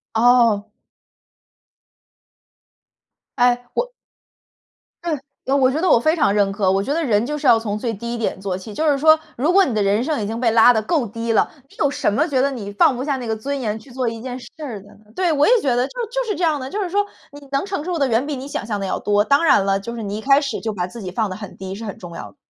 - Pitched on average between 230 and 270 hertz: Yes, high, 240 Hz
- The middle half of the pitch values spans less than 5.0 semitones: No, average, 5.3 semitones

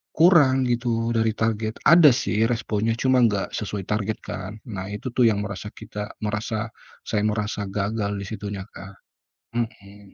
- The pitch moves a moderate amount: No, narrow, 2.3 semitones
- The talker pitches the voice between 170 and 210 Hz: No, low, 110 Hz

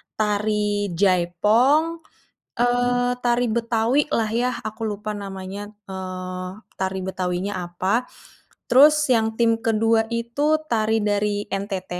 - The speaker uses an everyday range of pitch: Yes, average, 3.5 semitones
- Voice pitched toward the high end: Yes, high, 215 Hz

